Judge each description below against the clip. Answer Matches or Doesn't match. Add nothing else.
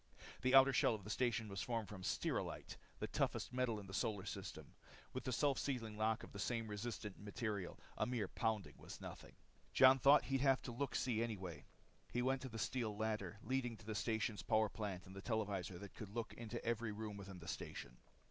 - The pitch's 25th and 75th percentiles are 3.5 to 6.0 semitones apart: Doesn't match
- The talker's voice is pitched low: Matches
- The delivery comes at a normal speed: Doesn't match